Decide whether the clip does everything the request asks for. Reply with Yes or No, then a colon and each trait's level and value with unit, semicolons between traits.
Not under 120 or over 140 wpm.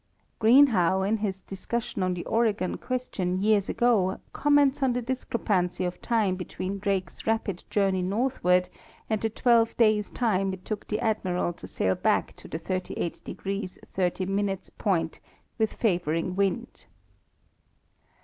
Yes: slow, 135 wpm